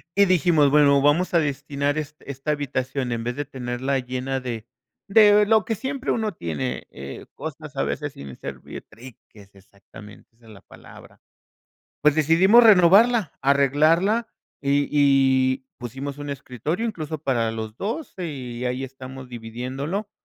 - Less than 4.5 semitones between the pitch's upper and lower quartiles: No, average, 5.1 semitones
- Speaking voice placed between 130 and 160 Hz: Yes, medium, 140 Hz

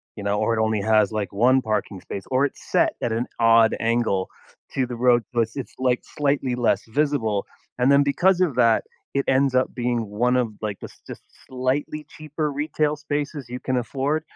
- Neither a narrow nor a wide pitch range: Yes, average, 4.0 semitones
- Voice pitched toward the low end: Yes, low, 125 Hz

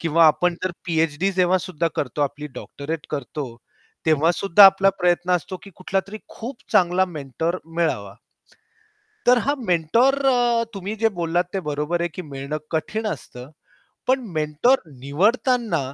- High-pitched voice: No, medium, 170 Hz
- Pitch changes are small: No, average, 4.4 semitones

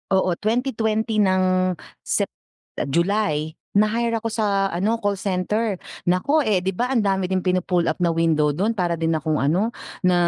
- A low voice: No, high, 190 Hz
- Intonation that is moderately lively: Yes, average, 3.7 semitones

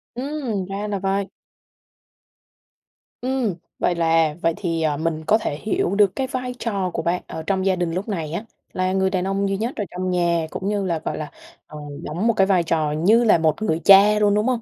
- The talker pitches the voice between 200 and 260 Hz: No, high, 190 Hz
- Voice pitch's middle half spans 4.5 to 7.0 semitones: No, average, 4.0 semitones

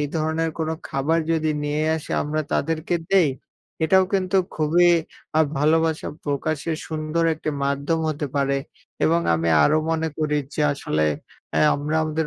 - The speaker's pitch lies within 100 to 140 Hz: No, medium, 155 Hz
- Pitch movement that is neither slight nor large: No, narrow, 1.7 semitones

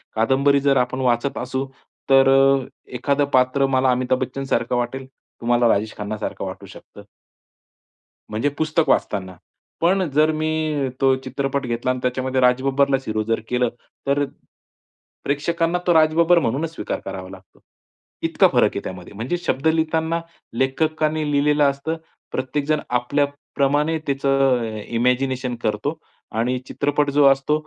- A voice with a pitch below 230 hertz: Yes, low, 135 Hz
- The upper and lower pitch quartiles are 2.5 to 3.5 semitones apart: Yes, average, 3.0 semitones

